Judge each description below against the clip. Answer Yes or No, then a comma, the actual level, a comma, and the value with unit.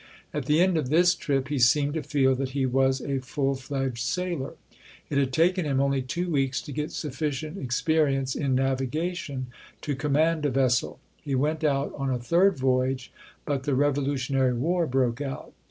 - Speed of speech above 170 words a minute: Yes, average, 180 wpm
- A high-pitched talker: No, medium, 140 Hz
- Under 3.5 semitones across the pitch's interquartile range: Yes, narrow, 2.6 semitones